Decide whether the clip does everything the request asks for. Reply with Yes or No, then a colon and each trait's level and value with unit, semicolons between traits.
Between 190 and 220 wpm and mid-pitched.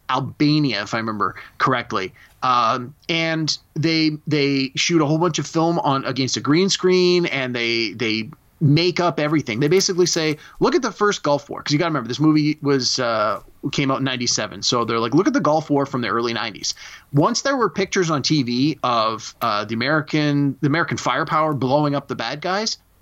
Yes: fast, 205 wpm; medium, 150 Hz